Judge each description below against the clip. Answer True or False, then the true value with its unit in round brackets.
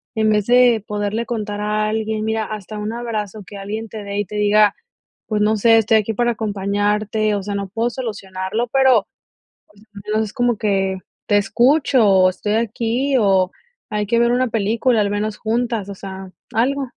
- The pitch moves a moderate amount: False (2.1 semitones)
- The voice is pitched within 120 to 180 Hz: False (215 Hz)